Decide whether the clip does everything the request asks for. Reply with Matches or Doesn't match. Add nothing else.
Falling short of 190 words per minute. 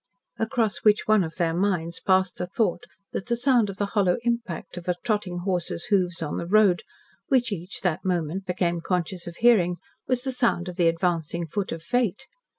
Doesn't match